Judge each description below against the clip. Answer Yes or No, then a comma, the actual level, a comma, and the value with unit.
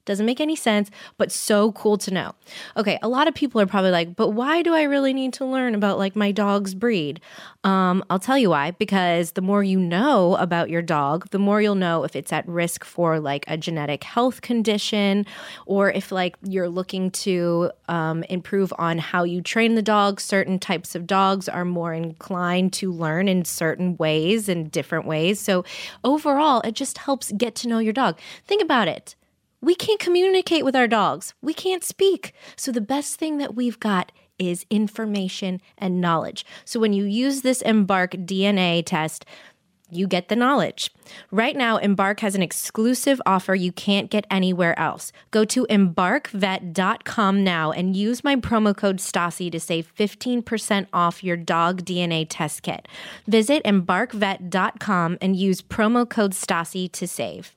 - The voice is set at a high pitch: Yes, high, 195 Hz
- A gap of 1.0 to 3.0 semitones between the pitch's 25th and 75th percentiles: No, average, 4.1 semitones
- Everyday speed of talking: Yes, average, 180 wpm